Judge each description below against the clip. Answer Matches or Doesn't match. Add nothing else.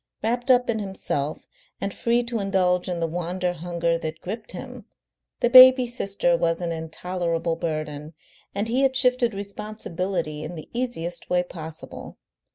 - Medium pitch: Matches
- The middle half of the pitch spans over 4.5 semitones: Matches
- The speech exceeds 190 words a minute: Doesn't match